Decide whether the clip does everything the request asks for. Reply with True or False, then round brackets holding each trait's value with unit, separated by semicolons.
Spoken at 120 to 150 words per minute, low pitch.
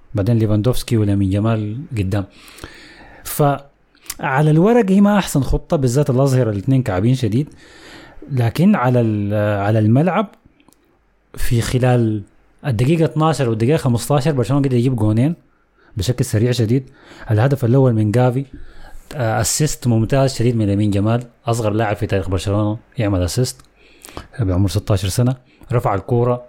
True (125 wpm; 120 Hz)